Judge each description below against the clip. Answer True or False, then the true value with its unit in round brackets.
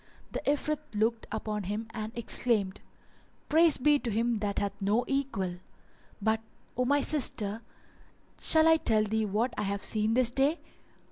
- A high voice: True (225 Hz)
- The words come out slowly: False (155 wpm)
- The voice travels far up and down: False (4.4 semitones)